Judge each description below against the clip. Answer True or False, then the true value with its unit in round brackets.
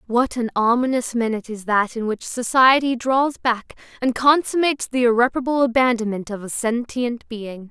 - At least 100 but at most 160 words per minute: True (155 wpm)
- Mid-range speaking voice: False (240 Hz)